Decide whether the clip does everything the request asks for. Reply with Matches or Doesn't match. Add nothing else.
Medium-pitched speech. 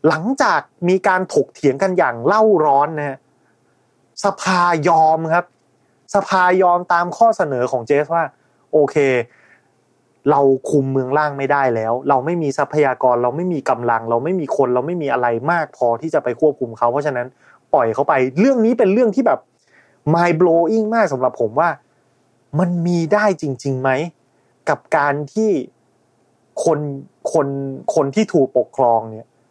Matches